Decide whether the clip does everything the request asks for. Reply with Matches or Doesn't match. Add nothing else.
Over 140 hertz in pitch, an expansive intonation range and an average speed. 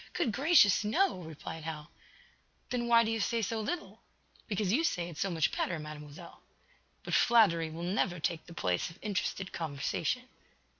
Matches